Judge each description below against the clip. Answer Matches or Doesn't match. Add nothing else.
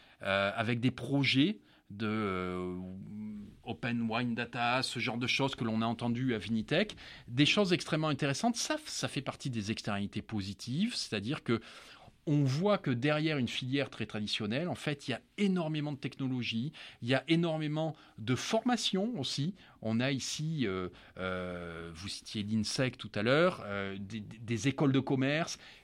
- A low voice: Matches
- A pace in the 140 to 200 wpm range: Matches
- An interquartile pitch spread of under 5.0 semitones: Doesn't match